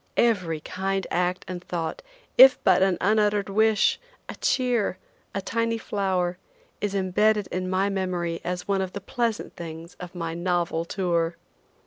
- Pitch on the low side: No, medium, 185 Hz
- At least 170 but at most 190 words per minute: No, average, 150 wpm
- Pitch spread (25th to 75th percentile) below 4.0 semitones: Yes, average, 2.8 semitones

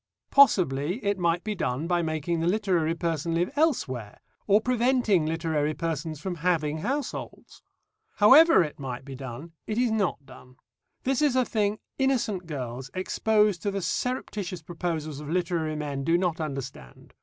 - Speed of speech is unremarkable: Yes, average, 155 wpm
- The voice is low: No, medium, 170 Hz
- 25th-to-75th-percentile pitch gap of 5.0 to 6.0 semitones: Yes, wide, 5.6 semitones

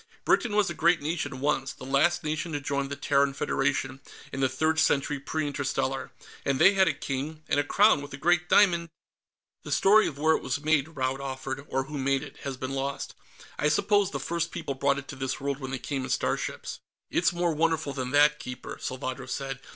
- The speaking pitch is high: No, medium, 140 Hz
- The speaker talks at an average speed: No, fast, 215 wpm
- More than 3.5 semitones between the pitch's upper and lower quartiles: No, average, 2.9 semitones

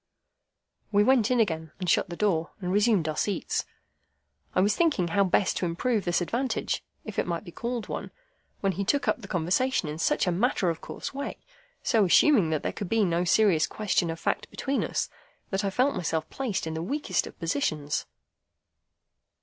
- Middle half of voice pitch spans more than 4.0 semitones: Yes, average, 5.2 semitones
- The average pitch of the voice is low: No, high, 195 Hz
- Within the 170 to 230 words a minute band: Yes, average, 190 wpm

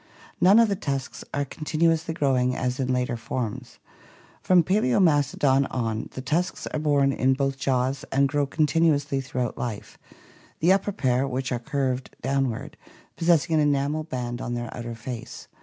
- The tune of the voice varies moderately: Yes, average, 3.4 semitones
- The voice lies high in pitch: No, low, 135 Hz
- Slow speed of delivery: No, average, 160 wpm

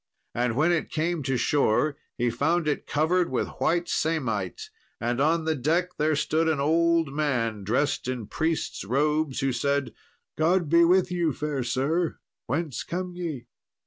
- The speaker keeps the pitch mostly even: No, average, 4.3 semitones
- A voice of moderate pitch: Yes, medium, 150 Hz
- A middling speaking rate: Yes, average, 160 wpm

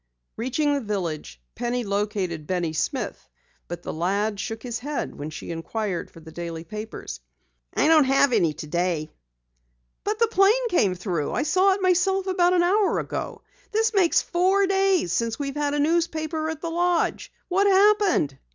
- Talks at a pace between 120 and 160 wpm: No, average, 170 wpm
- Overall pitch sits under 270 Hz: No, very high, 275 Hz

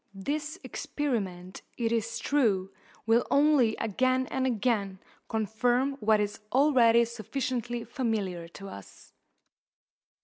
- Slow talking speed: Yes, slow, 105 wpm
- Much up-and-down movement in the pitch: No, average, 3.8 semitones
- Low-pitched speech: No, high, 230 Hz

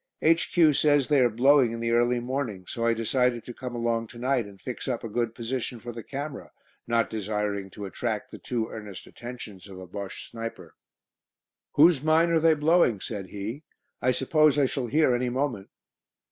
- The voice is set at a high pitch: No, low, 120 Hz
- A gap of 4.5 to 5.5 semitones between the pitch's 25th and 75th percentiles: No, average, 3.8 semitones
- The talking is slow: No, average, 190 wpm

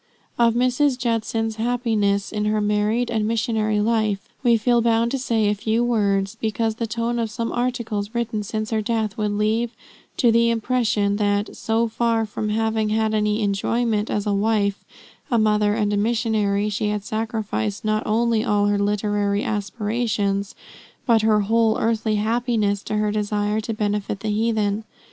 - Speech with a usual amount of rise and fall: No, narrow, 1.8 semitones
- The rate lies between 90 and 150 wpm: No, average, 165 wpm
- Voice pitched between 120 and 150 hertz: No, high, 215 Hz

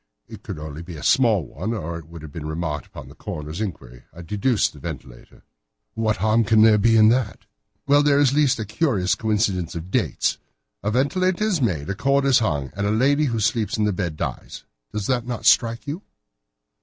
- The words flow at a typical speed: No, fast, 220 wpm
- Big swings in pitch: Yes, wide, 7.0 semitones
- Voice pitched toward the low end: Yes, low, 110 Hz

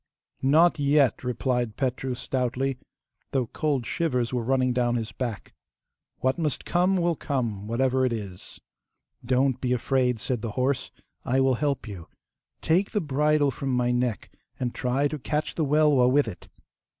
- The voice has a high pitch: No, low, 130 Hz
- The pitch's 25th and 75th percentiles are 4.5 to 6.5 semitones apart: No, average, 2.8 semitones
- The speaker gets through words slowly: No, average, 160 wpm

